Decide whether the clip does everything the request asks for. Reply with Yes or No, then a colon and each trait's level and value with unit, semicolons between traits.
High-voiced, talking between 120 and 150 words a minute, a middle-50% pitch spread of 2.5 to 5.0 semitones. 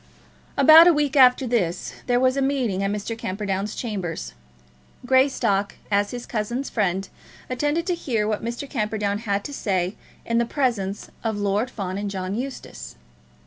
No: high, 220 Hz; average, 160 wpm; average, 4.5 semitones